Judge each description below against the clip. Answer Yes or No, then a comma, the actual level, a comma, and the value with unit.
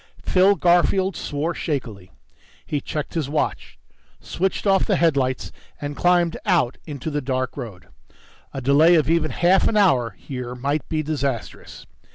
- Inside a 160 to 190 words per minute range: No, average, 150 wpm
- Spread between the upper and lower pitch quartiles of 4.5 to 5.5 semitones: Yes, average, 4.8 semitones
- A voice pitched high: No, medium, 150 Hz